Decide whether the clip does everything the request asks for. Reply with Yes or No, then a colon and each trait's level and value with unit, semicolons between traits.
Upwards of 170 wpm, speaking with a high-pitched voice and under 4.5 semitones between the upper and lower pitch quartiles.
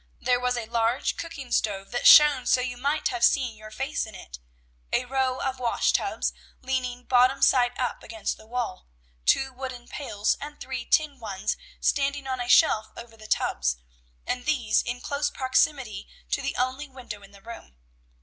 Yes: average, 180 wpm; very high, 250 Hz; average, 2.9 semitones